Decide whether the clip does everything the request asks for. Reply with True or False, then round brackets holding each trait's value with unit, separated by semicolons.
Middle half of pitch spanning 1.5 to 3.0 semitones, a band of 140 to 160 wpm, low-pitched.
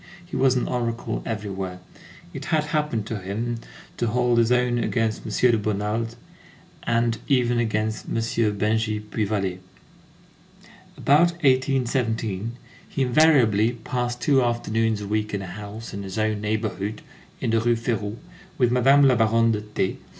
True (2.5 semitones; 150 wpm; 115 Hz)